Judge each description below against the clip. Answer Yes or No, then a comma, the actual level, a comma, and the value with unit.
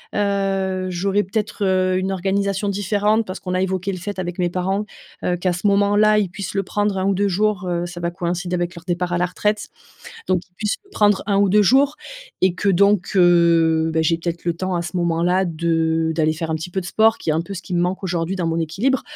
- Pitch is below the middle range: No, medium, 185 Hz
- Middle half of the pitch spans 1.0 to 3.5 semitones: Yes, narrow, 2.5 semitones